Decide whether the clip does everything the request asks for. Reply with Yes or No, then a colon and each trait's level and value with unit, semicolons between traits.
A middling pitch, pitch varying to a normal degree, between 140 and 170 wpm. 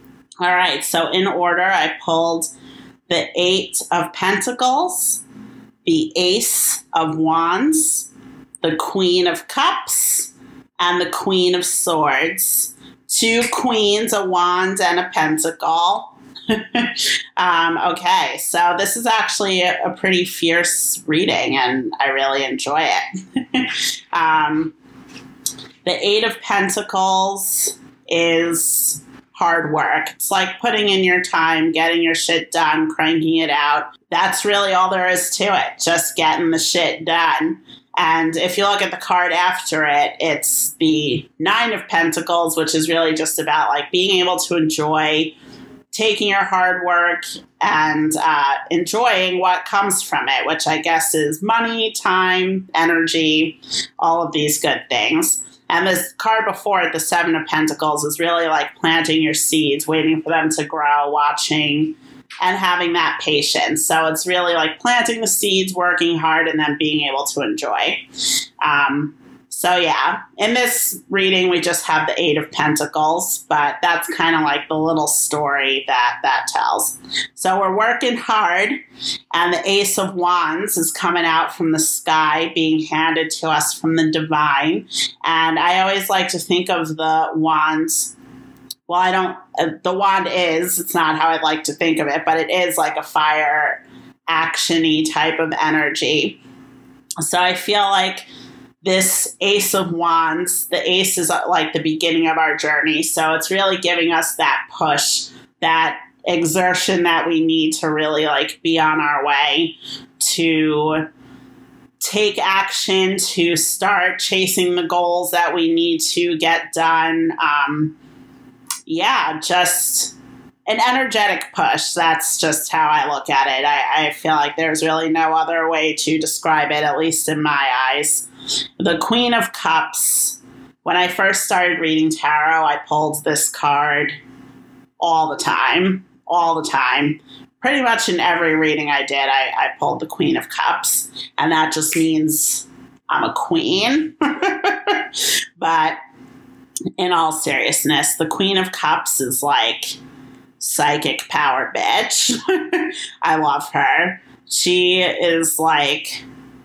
Yes: medium, 170 Hz; average, 3.4 semitones; average, 150 wpm